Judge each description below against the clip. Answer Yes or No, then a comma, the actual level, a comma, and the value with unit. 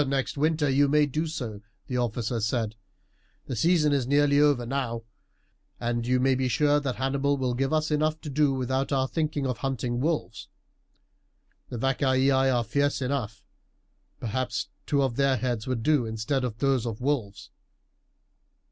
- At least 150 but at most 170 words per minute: Yes, average, 165 wpm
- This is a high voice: No, low, 130 Hz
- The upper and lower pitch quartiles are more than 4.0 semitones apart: No, average, 2.9 semitones